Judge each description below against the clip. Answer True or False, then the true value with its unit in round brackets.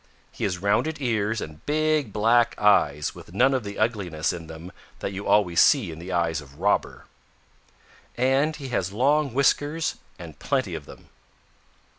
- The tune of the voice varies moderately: False (7.3 semitones)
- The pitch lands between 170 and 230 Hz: False (105 Hz)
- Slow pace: False (165 wpm)